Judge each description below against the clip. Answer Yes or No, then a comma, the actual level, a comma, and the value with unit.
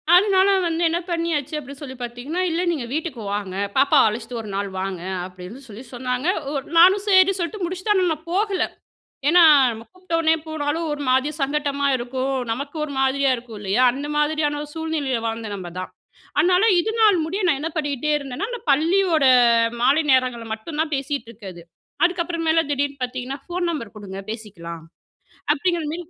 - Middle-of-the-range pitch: No, very high, 290 Hz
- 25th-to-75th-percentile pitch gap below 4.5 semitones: No, wide, 5.5 semitones